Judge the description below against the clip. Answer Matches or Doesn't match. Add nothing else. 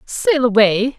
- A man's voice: Doesn't match